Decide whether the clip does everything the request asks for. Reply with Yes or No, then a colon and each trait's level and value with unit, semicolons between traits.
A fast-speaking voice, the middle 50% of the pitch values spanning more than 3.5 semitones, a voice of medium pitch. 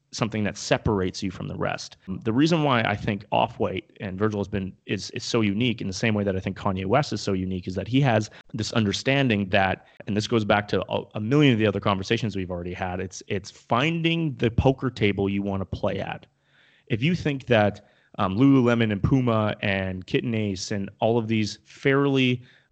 No: fast, 215 wpm; average, 3.9 semitones; low, 110 Hz